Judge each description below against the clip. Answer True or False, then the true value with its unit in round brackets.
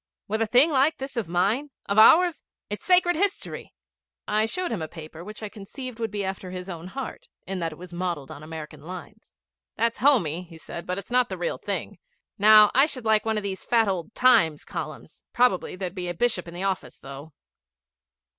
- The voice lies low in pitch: False (205 Hz)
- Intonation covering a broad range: True (5.7 semitones)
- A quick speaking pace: True (210 wpm)